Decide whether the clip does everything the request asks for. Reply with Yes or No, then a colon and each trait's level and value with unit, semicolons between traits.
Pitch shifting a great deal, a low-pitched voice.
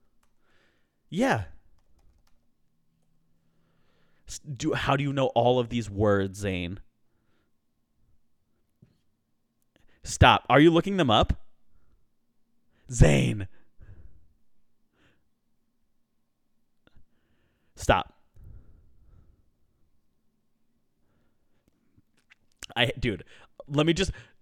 Yes: wide, 6.7 semitones; low, 100 Hz